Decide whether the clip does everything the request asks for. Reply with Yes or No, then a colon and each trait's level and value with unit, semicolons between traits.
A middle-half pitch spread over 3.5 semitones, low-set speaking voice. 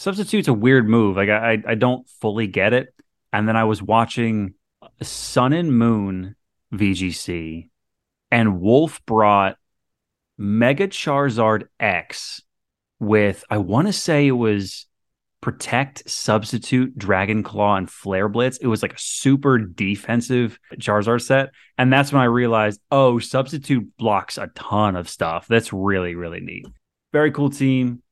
Yes: average, 4.2 semitones; low, 115 Hz